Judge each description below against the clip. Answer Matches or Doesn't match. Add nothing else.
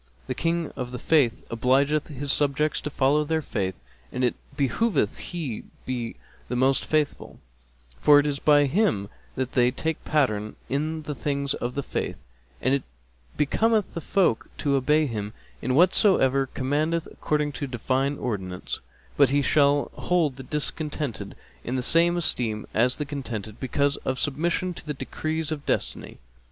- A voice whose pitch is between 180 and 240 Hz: Doesn't match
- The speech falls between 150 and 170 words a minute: Matches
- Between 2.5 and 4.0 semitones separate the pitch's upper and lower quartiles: Matches